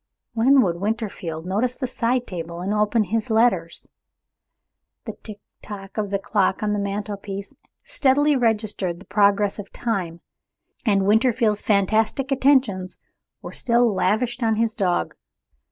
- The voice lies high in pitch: Yes, high, 210 Hz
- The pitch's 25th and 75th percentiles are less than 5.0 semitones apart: Yes, average, 3.0 semitones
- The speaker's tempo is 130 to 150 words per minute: Yes, average, 140 wpm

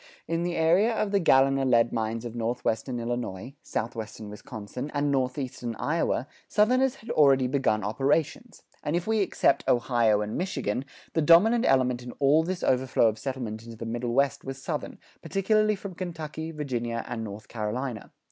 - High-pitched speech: No, low, 130 Hz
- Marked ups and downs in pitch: Yes, wide, 5.8 semitones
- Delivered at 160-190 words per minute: Yes, average, 165 wpm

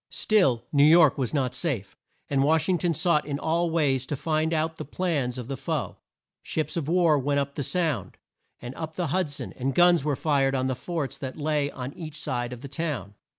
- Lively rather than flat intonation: No, average, 3.4 semitones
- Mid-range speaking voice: Yes, medium, 145 Hz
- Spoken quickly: Yes, fast, 220 wpm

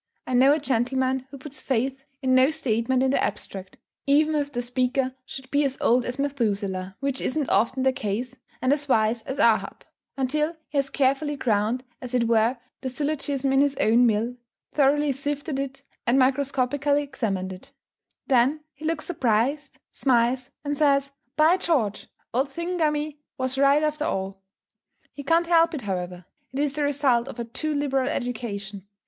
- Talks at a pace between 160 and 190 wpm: Yes, average, 170 wpm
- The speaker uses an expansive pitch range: No, average, 3.1 semitones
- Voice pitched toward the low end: No, very high, 265 Hz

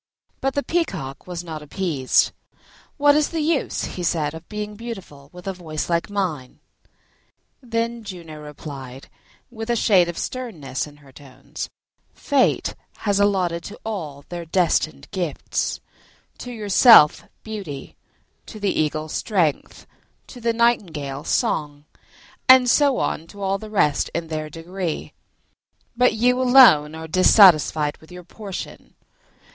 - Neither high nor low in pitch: Yes, medium, 180 Hz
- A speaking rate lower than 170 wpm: Yes, average, 140 wpm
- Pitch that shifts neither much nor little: No, wide, 6.5 semitones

